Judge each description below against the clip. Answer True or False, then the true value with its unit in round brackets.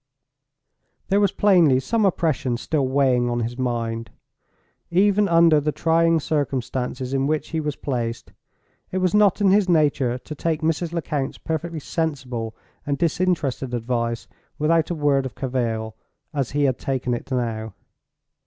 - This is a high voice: False (140 Hz)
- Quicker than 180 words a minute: False (150 wpm)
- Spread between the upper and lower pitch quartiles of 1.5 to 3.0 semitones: False (5.0 semitones)